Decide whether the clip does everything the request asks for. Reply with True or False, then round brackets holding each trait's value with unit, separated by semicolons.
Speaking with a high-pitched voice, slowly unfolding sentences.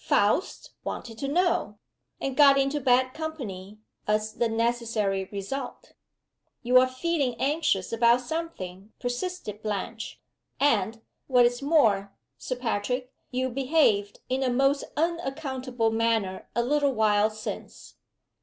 True (245 Hz; 125 wpm)